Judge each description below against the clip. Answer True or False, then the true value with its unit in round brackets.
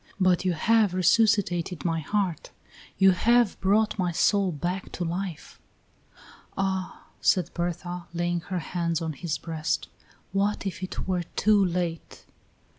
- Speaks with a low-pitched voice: False (180 Hz)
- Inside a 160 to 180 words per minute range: False (135 wpm)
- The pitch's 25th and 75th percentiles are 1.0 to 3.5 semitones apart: True (2.4 semitones)